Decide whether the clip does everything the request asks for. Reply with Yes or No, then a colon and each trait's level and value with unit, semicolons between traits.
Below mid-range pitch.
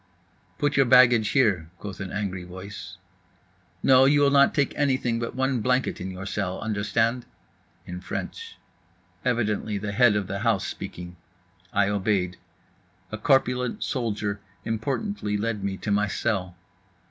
Yes: low, 110 Hz